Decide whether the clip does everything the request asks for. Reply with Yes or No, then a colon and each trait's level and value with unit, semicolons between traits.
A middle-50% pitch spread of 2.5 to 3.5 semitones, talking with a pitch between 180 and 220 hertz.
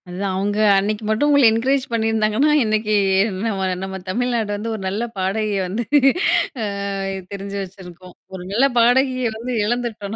Yes: average, 3.2 semitones; high, 215 Hz